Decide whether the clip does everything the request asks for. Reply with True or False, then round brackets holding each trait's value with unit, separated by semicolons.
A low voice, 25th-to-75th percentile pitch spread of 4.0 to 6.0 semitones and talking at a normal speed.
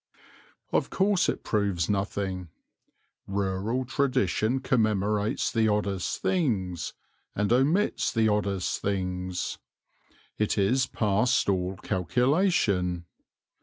False (105 Hz; 4.8 semitones; 90 wpm)